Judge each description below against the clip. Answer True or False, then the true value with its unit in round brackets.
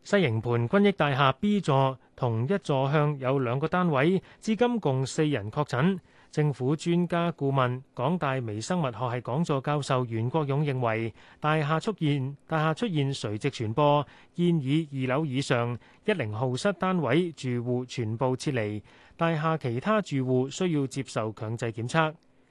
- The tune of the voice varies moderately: True (4.3 semitones)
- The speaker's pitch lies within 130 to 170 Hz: True (140 Hz)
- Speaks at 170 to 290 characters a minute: True (245 characters per minute)